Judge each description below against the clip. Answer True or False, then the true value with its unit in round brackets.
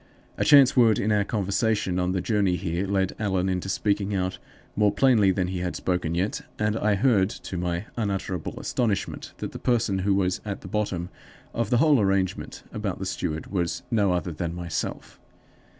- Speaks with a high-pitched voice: False (95 Hz)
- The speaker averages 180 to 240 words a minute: True (185 wpm)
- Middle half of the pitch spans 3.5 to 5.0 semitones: False (2.8 semitones)